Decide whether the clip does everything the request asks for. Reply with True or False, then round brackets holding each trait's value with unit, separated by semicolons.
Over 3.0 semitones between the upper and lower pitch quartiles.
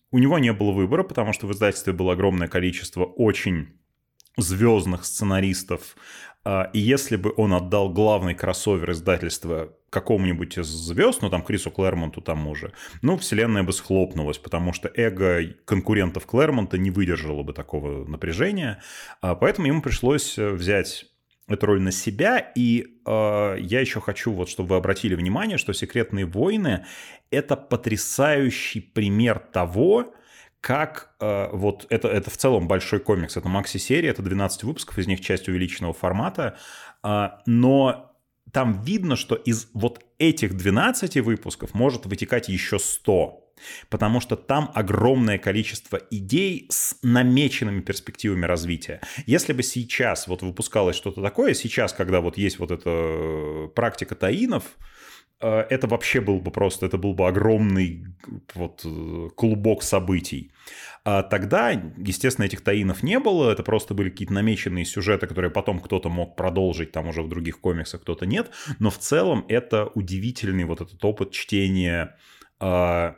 True (3.9 semitones)